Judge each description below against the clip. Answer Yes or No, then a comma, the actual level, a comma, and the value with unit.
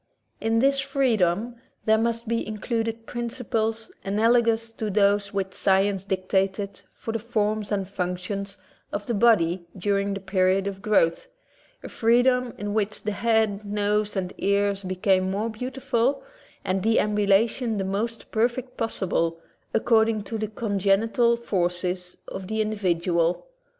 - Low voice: No, high, 210 Hz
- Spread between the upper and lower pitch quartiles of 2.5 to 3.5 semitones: Yes, average, 2.8 semitones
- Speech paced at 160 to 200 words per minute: No, slow, 135 wpm